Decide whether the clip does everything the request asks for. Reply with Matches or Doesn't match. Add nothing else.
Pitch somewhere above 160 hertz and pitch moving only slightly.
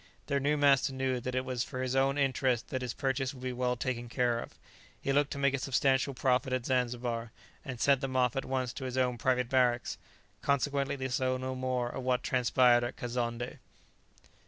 Doesn't match